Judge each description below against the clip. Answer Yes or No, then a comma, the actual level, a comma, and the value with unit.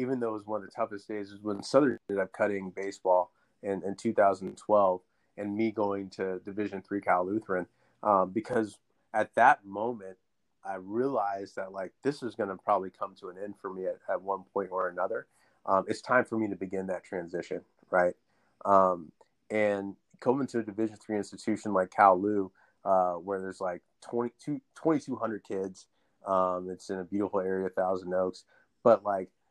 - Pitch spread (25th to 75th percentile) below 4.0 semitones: Yes, narrow, 2.4 semitones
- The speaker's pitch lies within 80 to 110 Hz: Yes, low, 100 Hz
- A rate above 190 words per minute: No, average, 180 wpm